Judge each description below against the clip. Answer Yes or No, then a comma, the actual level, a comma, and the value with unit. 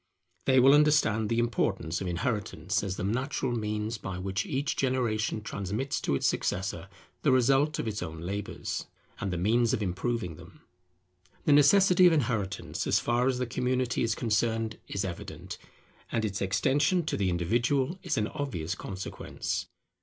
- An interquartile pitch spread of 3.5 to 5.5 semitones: Yes, average, 5.2 semitones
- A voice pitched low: Yes, low, 115 Hz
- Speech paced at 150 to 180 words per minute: Yes, average, 160 wpm